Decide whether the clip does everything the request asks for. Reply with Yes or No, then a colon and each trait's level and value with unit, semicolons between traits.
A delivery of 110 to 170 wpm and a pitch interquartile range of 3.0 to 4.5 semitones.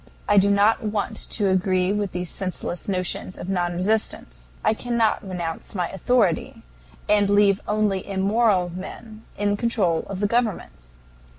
No: average, 150 wpm; narrow, 2.6 semitones